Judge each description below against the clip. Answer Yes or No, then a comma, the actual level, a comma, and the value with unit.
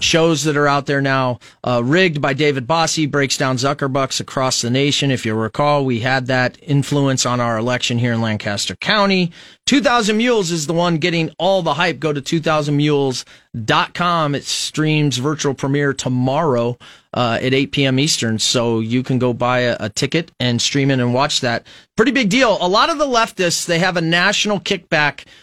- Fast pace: No, average, 190 wpm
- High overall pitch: No, medium, 140 Hz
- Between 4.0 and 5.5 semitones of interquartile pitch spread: Yes, average, 4.7 semitones